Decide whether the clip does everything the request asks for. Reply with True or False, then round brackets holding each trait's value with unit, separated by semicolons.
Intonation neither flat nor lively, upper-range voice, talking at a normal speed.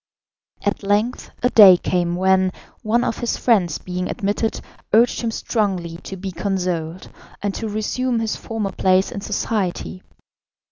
True (3.4 semitones; 200 Hz; 145 wpm)